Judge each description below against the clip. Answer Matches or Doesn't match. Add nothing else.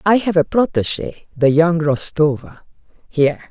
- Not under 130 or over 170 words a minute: Matches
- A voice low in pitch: Doesn't match